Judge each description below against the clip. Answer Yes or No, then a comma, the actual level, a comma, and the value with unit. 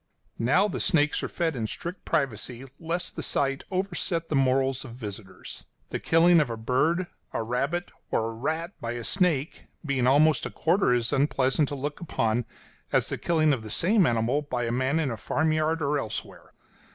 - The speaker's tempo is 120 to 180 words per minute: No, average, 190 wpm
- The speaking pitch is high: No, medium, 140 Hz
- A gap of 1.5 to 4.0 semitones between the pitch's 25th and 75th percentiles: No, average, 5.2 semitones